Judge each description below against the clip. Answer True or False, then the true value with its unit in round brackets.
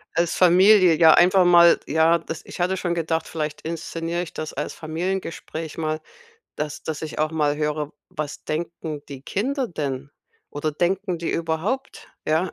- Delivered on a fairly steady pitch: True (2.3 semitones)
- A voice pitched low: False (165 Hz)